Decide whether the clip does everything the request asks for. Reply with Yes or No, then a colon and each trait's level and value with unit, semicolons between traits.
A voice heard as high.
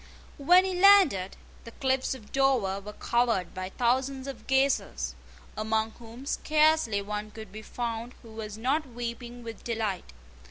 Yes: high, 235 Hz